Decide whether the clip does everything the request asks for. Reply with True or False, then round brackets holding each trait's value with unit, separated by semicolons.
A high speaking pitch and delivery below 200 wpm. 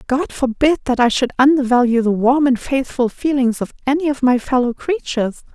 True (260 Hz; 185 wpm)